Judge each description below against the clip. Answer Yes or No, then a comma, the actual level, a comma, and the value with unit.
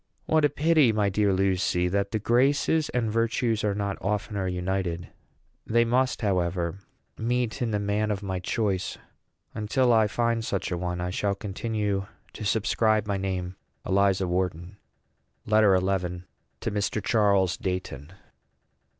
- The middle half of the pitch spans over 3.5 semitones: No, average, 3.0 semitones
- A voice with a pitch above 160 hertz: No, low, 100 Hz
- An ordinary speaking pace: Yes, average, 150 wpm